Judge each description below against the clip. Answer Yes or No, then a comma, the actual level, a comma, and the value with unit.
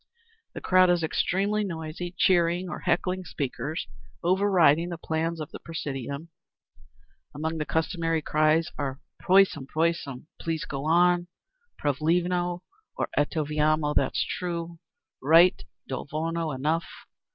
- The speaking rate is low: Yes, slow, 120 wpm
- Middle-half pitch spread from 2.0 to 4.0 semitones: Yes, narrow, 2.4 semitones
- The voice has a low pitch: No, medium, 165 Hz